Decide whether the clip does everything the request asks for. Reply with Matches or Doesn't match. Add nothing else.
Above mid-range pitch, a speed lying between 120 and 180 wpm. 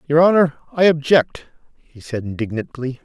Doesn't match